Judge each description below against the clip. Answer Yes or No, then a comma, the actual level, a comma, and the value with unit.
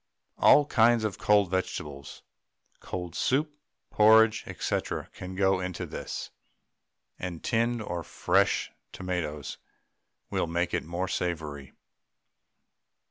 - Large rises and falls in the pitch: No, average, 4.3 semitones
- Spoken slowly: Yes, slow, 105 wpm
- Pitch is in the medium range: No, very low, 95 Hz